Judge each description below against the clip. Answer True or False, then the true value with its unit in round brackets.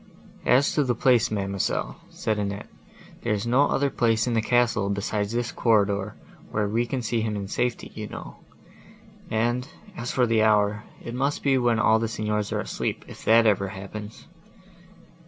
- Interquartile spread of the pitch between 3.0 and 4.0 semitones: False (2.5 semitones)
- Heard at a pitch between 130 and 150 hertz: False (110 Hz)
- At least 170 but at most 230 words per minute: True (175 wpm)